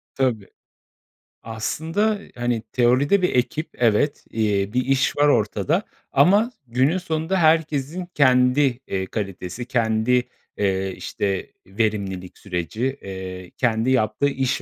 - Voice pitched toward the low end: Yes, low, 125 Hz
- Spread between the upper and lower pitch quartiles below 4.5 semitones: No, wide, 5.6 semitones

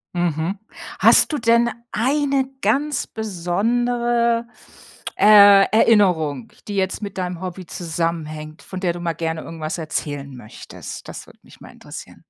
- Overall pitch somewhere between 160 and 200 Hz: Yes, high, 190 Hz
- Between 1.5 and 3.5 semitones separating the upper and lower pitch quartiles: No, wide, 5.9 semitones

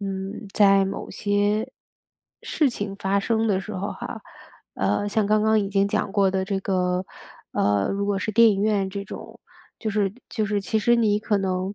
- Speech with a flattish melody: Yes, narrow, 1.6 semitones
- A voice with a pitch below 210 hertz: Yes, high, 200 Hz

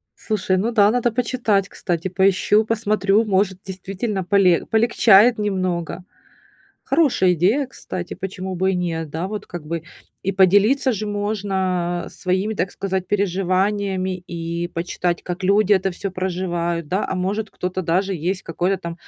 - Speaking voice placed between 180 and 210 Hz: Yes, high, 190 Hz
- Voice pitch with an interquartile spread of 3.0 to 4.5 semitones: No, narrow, 2.5 semitones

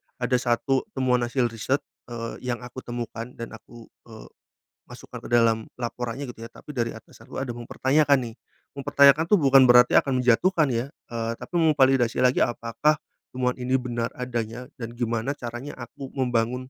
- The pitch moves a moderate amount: No, narrow, 2.2 semitones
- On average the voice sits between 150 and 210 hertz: No, low, 125 Hz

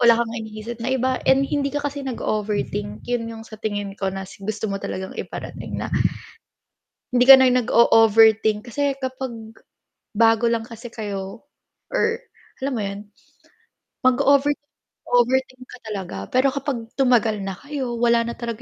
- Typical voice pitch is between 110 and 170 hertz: No, high, 235 Hz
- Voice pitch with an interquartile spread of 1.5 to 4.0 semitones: Yes, average, 3.2 semitones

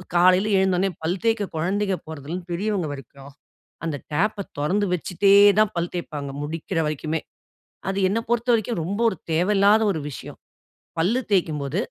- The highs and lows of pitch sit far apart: No, average, 4.3 semitones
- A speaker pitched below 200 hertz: Yes, medium, 185 Hz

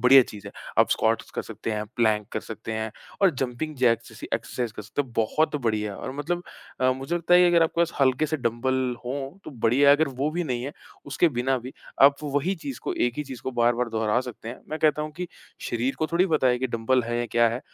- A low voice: Yes, low, 130 Hz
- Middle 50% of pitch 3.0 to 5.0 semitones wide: Yes, average, 4.2 semitones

